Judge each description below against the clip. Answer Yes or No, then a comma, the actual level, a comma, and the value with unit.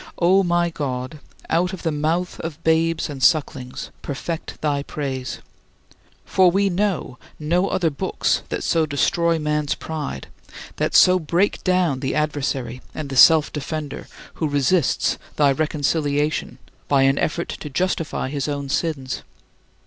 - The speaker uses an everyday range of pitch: Yes, average, 3.2 semitones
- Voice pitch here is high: No, medium, 155 Hz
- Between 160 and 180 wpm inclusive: No, average, 140 wpm